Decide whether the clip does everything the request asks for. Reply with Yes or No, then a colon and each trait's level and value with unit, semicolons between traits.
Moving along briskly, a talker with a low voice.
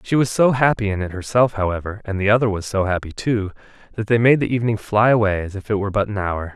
Yes: fast, 265 wpm; low, 105 Hz